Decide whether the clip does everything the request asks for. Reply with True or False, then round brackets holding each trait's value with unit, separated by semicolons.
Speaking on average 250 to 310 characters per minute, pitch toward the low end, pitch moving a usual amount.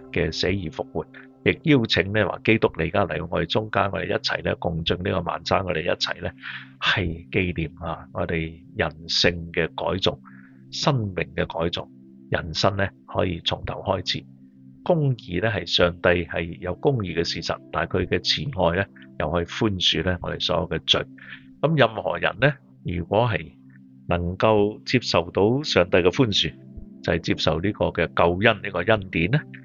False (255 characters per minute; 85 Hz; 6.8 semitones)